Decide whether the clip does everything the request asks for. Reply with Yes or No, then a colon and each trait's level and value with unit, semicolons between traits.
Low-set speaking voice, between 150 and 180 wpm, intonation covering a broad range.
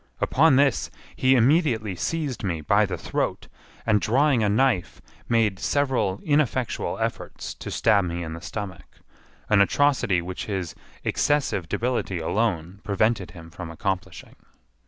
No: low, 105 Hz; slow, 135 wpm; wide, 6.2 semitones